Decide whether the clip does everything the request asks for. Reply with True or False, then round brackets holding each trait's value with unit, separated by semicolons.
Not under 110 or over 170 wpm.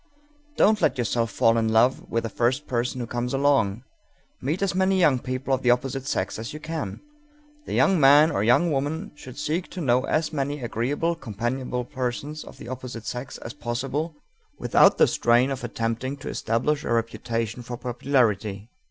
False (180 wpm)